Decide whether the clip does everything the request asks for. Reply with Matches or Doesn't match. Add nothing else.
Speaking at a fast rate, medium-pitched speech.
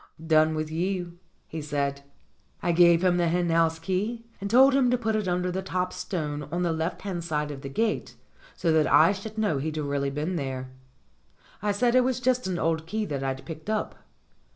Matches